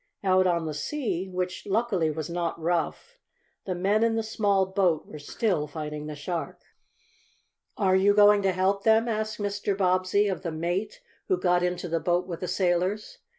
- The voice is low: No, medium, 185 Hz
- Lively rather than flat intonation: No, average, 3.0 semitones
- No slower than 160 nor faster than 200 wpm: Yes, average, 180 wpm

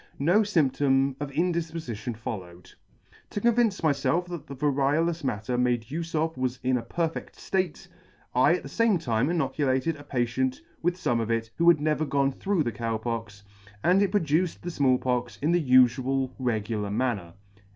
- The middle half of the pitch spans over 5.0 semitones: Yes, wide, 5.4 semitones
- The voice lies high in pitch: No, low, 135 Hz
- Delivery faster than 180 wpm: No, average, 170 wpm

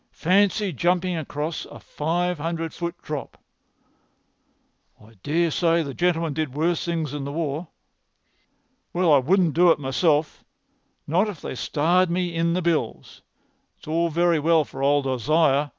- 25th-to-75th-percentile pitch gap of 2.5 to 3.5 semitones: Yes, average, 2.8 semitones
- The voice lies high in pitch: No, medium, 165 Hz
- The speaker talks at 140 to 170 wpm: Yes, average, 150 wpm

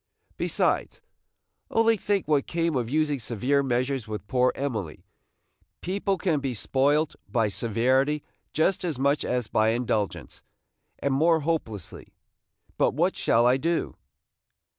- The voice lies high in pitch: No, low, 135 Hz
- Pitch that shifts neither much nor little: Yes, average, 4.9 semitones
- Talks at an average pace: No, slow, 130 wpm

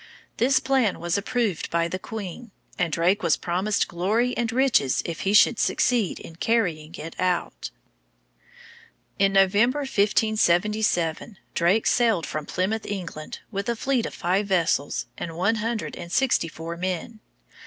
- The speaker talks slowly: No, average, 145 wpm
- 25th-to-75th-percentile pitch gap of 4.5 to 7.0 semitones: Yes, average, 4.8 semitones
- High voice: Yes, high, 195 Hz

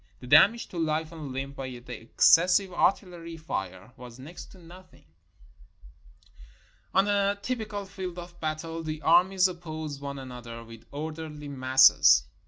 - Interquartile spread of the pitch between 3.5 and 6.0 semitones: Yes, average, 5.1 semitones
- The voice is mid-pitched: Yes, medium, 160 Hz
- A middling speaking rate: Yes, average, 150 wpm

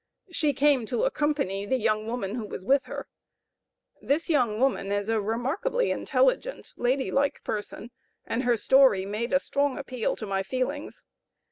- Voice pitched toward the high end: Yes, very high, 255 Hz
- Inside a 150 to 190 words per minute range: Yes, average, 160 wpm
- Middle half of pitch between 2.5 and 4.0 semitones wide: No, average, 4.9 semitones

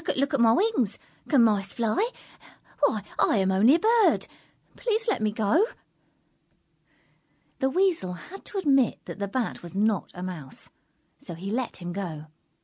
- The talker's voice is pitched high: Yes, high, 225 Hz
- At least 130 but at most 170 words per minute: Yes, average, 160 wpm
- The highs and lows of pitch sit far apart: Yes, wide, 7.9 semitones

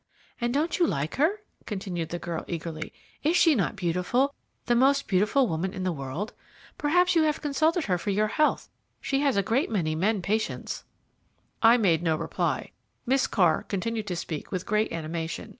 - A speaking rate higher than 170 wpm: Yes, average, 180 wpm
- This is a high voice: Yes, high, 210 Hz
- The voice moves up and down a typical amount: No, wide, 8.0 semitones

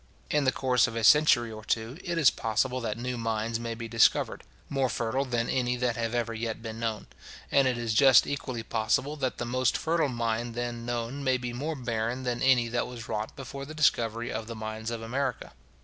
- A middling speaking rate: No, fast, 215 wpm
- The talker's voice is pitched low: Yes, low, 120 Hz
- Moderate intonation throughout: No, narrow, 2.3 semitones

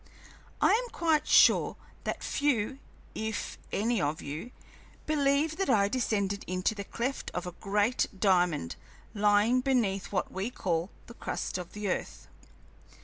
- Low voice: No, high, 210 Hz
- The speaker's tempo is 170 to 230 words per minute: No, average, 145 wpm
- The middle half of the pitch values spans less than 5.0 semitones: No, average, 5.3 semitones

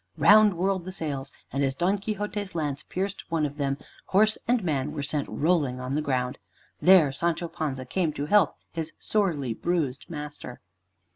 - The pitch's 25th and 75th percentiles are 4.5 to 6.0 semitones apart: Yes, average, 5.2 semitones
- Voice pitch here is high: No, medium, 155 Hz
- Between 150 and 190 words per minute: Yes, average, 170 wpm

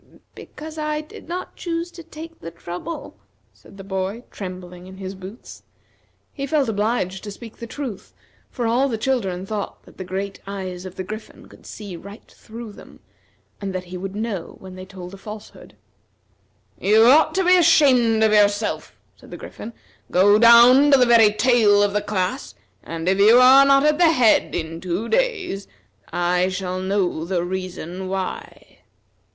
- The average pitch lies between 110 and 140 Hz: No, high, 205 Hz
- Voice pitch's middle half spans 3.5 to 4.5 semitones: No, average, 5.2 semitones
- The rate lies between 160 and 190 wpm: Yes, average, 175 wpm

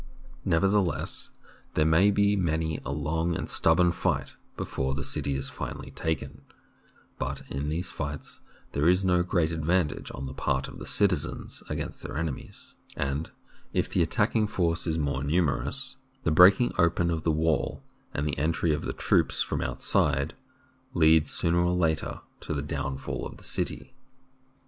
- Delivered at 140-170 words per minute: Yes, average, 165 wpm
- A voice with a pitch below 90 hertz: Yes, very low, 80 Hz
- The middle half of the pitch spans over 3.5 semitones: No, average, 3.2 semitones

